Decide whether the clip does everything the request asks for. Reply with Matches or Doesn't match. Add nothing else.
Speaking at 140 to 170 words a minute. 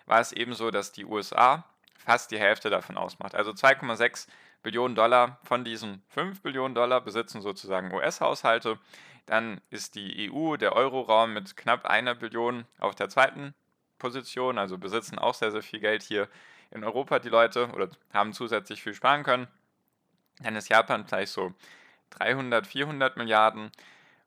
Matches